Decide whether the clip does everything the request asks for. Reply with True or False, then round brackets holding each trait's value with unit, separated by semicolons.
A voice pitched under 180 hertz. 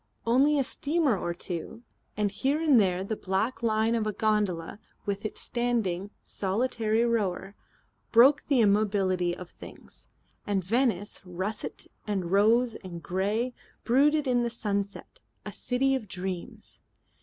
False (215 Hz)